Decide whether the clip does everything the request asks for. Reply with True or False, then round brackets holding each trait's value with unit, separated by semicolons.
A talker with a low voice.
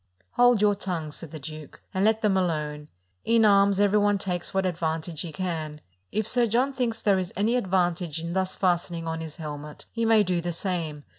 False (185 Hz)